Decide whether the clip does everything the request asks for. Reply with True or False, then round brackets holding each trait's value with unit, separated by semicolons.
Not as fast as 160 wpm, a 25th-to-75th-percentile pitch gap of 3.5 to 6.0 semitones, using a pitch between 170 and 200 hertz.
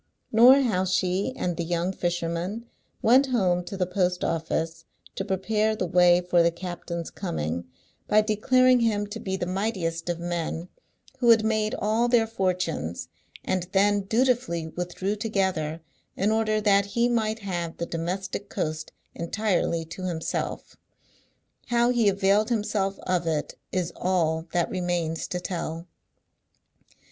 True (145 wpm; 4.0 semitones; 185 Hz)